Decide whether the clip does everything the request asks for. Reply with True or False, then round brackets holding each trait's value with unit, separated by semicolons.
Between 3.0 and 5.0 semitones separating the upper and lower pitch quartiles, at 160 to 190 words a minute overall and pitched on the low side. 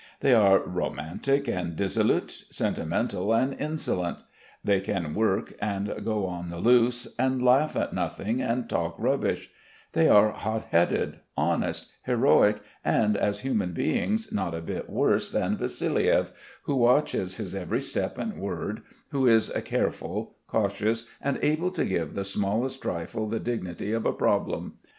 False (4.6 semitones; 150 wpm; 105 Hz)